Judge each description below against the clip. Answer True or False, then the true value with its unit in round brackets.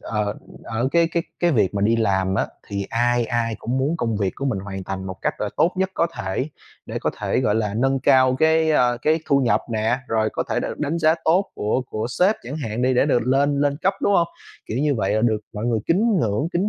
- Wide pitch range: True (5.9 semitones)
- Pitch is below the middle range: True (125 Hz)